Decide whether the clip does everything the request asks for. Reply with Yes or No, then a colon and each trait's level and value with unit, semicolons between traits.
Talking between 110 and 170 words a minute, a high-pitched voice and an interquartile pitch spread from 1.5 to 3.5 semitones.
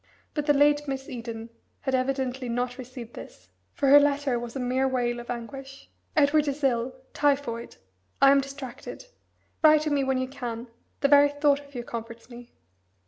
No: average, 180 wpm; very high, 265 Hz; average, 2.8 semitones